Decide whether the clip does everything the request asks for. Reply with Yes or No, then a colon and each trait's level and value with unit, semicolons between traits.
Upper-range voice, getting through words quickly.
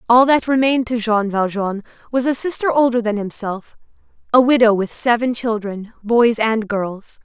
No: high, 230 Hz; average, 155 wpm